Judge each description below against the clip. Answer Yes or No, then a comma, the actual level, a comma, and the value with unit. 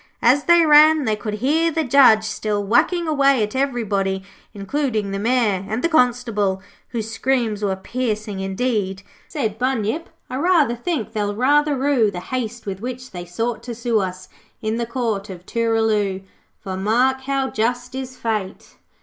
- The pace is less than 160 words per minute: No, average, 165 wpm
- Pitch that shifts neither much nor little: Yes, average, 4.2 semitones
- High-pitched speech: Yes, high, 230 Hz